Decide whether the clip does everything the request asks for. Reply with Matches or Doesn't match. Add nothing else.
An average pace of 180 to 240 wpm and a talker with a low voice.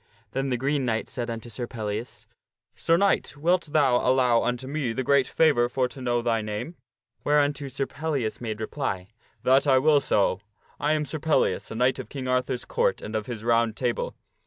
Matches